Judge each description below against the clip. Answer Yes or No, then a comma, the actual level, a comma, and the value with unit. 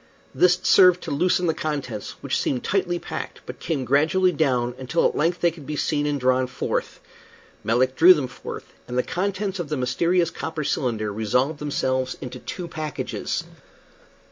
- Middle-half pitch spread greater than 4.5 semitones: Yes, average, 5.2 semitones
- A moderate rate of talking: Yes, average, 170 wpm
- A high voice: No, medium, 150 Hz